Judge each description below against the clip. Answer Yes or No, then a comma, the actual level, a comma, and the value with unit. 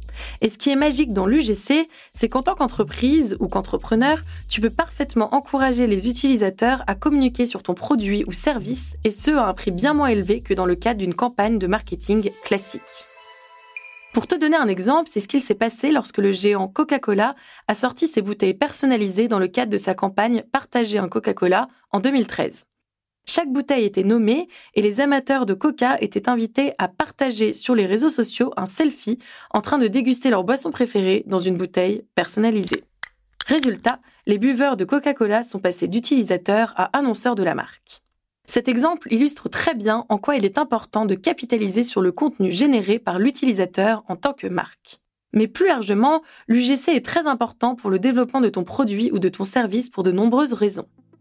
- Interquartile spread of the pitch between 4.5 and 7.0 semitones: Yes, average, 5.2 semitones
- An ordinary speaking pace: Yes, average, 185 wpm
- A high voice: Yes, high, 235 Hz